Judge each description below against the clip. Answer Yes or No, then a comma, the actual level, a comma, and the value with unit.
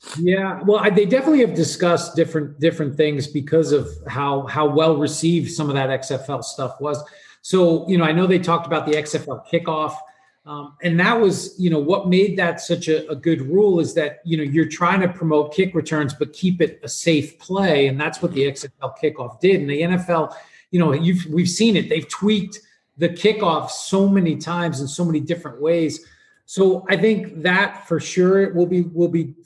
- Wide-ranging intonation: No, average, 3.3 semitones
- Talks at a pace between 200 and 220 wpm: Yes, fast, 205 wpm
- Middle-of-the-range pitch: Yes, medium, 165 Hz